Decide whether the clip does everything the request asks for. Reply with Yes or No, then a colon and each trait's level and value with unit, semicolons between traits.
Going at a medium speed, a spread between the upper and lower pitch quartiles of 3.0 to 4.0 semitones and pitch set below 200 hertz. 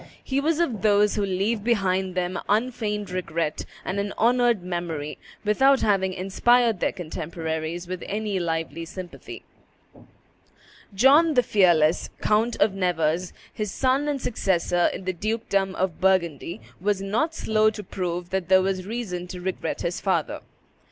Yes: average, 145 wpm; average, 3.6 semitones; high, 190 Hz